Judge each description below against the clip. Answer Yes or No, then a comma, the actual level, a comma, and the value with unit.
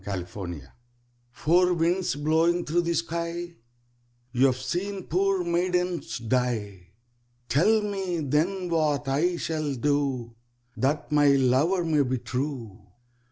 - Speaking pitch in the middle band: Yes, medium, 155 Hz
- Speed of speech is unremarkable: No, slow, 120 wpm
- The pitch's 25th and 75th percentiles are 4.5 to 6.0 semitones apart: Yes, average, 5.0 semitones